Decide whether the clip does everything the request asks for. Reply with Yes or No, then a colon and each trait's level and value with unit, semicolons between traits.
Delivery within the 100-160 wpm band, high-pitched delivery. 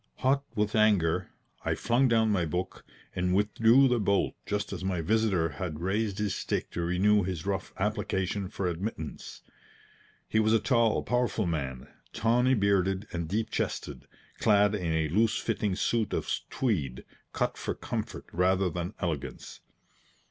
No: average, 155 wpm; low, 100 Hz